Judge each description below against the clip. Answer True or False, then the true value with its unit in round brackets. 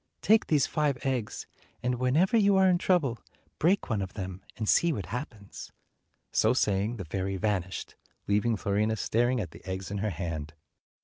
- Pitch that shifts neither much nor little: False (5.9 semitones)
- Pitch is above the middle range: False (110 Hz)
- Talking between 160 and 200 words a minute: True (175 wpm)